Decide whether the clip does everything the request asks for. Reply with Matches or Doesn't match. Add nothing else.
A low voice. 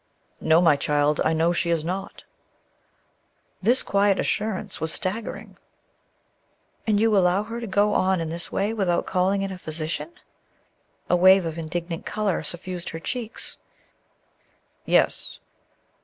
Doesn't match